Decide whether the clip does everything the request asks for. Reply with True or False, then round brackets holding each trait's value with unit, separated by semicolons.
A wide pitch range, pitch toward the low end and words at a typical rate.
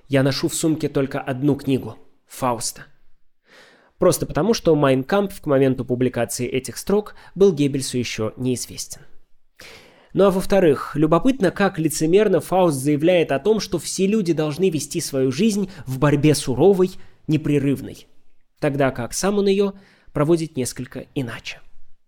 False (5.8 semitones; 150 Hz; 135 wpm)